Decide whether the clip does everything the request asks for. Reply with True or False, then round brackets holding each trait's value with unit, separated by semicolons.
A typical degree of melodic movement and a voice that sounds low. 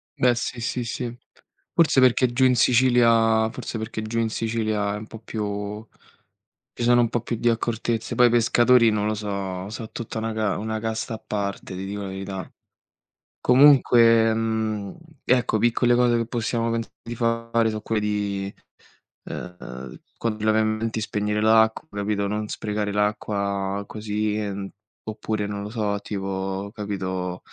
False (2.1 semitones; 110 Hz)